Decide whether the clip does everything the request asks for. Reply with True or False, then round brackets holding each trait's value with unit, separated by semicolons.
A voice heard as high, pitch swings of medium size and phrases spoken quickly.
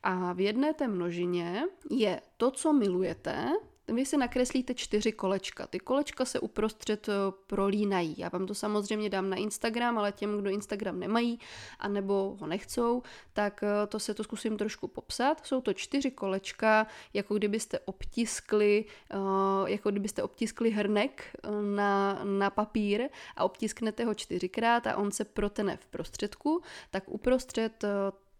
False (210 Hz; 3.1 semitones; 140 wpm)